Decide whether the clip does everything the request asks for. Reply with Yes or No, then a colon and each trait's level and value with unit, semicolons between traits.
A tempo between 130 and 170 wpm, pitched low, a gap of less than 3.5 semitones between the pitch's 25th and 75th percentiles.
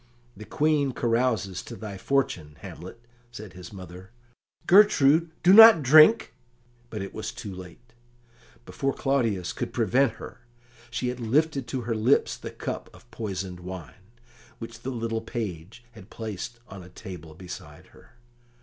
No: average, 160 wpm; low, 115 Hz; wide, 5.4 semitones